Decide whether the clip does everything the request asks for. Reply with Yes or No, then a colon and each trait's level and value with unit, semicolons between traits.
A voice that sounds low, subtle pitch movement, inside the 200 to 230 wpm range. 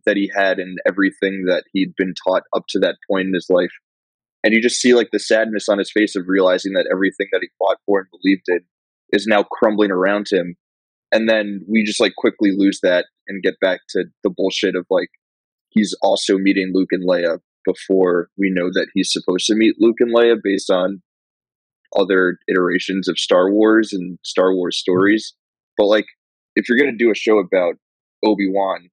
Yes: very low, 95 Hz; narrow, 2.3 semitones; fast, 205 wpm